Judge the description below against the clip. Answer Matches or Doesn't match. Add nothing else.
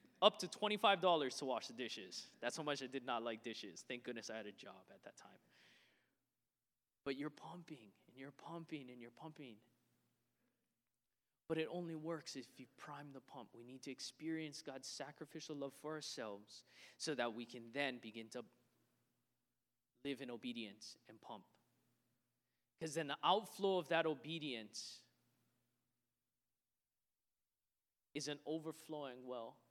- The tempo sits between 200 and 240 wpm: Doesn't match